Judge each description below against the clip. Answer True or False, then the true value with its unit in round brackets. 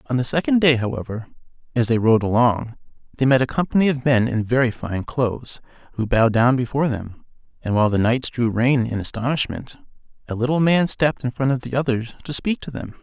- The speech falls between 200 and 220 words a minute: True (205 wpm)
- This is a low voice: True (125 Hz)